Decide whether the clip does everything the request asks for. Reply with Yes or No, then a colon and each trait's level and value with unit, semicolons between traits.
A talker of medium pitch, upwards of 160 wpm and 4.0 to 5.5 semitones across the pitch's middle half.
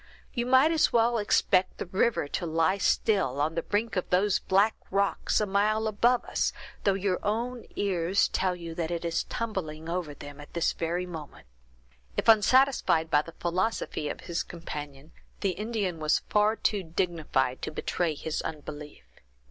Yes: medium, 180 Hz; average, 170 wpm; average, 4.6 semitones